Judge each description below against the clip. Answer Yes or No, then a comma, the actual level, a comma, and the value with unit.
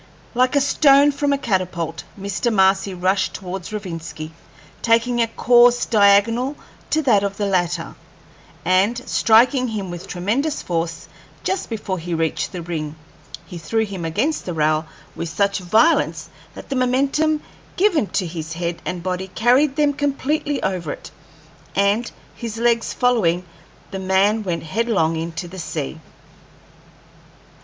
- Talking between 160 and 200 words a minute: No, average, 145 wpm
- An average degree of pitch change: No, wide, 5.9 semitones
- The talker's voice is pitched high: Yes, high, 200 Hz